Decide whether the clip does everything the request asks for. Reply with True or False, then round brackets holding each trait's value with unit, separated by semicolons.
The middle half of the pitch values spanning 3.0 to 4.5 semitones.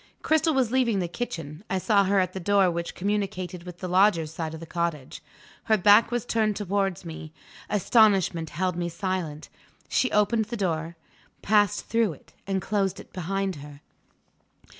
True (3.6 semitones)